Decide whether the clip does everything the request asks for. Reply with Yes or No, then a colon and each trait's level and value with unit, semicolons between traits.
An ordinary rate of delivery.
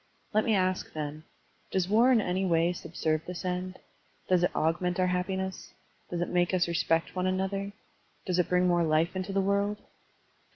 Yes: average, 190 wpm